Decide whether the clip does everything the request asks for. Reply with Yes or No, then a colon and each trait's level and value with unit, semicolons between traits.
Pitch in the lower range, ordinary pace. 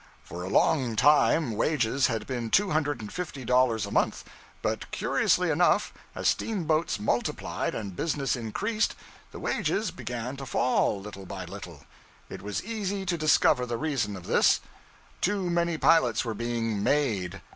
Yes: low, 125 Hz; average, 155 wpm